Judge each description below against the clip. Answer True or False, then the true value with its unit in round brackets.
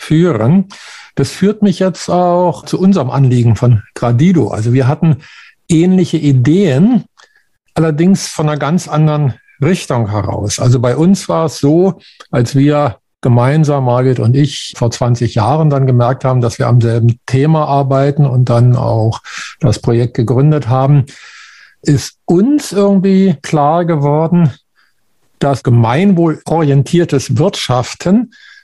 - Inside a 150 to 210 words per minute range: False (130 wpm)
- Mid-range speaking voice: True (145 Hz)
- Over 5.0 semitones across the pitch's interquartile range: True (5.5 semitones)